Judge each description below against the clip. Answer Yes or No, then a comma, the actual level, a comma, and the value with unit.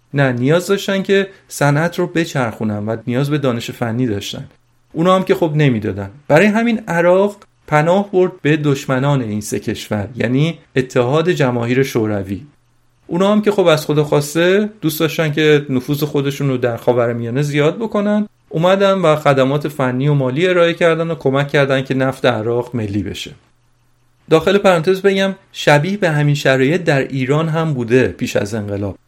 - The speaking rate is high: Yes, fast, 165 wpm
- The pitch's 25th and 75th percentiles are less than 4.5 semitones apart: No, wide, 5.4 semitones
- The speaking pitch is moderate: Yes, medium, 145 Hz